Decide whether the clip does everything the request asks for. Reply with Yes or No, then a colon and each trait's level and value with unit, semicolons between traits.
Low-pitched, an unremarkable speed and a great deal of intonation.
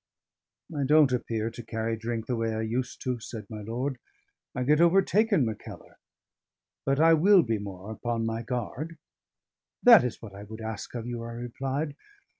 No: low, 120 Hz; average, 175 wpm; average, 4.1 semitones